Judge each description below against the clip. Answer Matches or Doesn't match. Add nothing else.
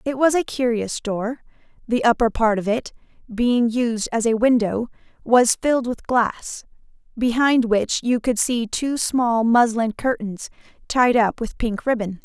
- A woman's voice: Matches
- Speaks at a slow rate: Doesn't match